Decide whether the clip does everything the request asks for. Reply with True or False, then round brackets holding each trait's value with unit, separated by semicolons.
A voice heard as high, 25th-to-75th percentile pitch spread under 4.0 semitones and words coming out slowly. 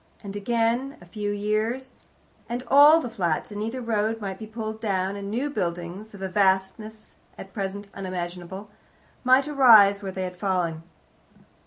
False (205 Hz; 3.1 semitones; 160 wpm)